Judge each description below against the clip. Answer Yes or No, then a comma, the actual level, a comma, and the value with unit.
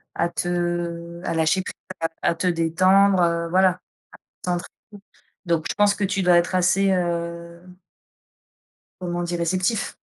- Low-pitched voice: No, medium, 175 Hz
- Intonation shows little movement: Yes, narrow, 1.6 semitones